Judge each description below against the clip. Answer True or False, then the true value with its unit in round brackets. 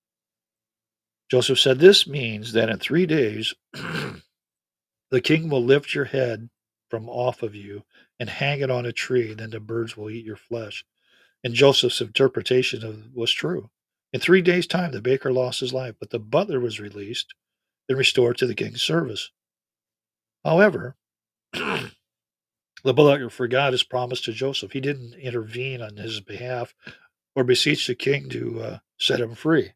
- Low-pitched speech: True (125 Hz)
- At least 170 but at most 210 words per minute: False (160 wpm)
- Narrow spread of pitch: False (3.3 semitones)